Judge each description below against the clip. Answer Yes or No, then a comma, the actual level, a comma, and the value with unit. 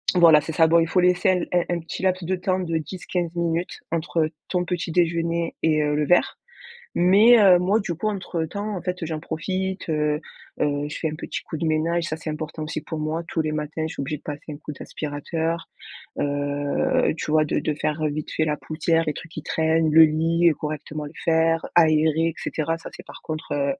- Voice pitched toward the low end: No, medium, 160 Hz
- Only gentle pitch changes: Yes, narrow, 2.3 semitones